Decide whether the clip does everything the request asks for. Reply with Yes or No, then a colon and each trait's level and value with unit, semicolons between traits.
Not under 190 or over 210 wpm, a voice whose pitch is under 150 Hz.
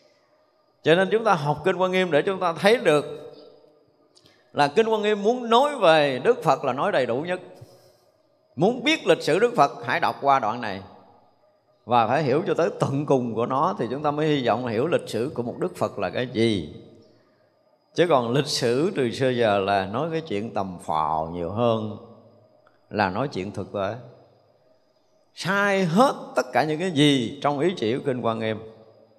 Yes: average, 200 wpm; medium, 140 Hz